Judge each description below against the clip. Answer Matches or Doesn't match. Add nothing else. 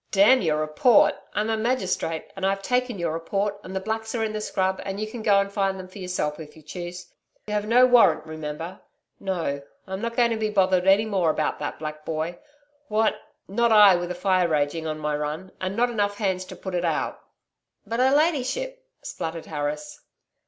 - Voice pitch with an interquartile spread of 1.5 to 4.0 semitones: Doesn't match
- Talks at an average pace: Doesn't match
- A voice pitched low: Doesn't match